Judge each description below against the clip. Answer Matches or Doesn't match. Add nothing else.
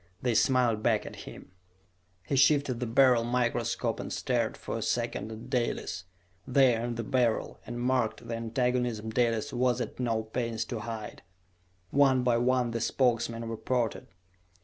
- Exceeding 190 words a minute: Doesn't match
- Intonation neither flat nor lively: Doesn't match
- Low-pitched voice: Matches